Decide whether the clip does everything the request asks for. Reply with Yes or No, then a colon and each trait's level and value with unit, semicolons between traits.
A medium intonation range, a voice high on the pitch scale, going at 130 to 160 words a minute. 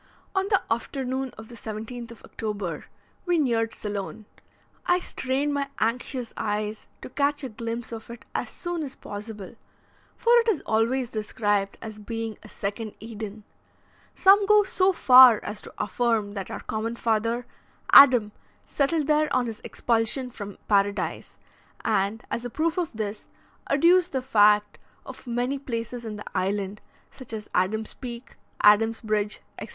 Yes: average, 3.9 semitones; high, 230 Hz; average, 155 wpm